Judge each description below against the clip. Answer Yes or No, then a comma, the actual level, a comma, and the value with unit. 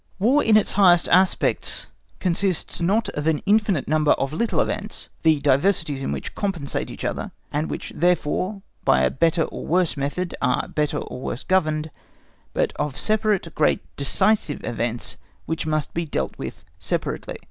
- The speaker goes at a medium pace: Yes, average, 160 wpm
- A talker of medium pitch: Yes, medium, 165 Hz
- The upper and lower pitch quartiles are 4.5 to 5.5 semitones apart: Yes, average, 4.8 semitones